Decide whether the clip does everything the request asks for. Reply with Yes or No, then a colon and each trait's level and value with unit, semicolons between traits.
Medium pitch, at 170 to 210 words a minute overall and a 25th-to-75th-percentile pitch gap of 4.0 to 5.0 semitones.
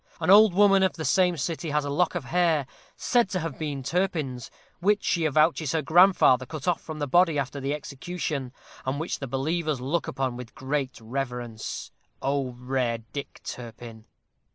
Yes: medium, 150 Hz; average, 175 wpm; average, 4.7 semitones